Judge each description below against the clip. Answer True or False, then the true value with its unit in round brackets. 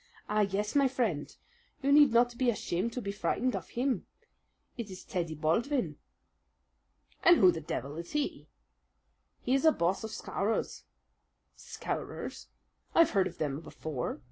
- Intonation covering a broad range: True (6.9 semitones)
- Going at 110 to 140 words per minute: False (150 wpm)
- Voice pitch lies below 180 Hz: False (210 Hz)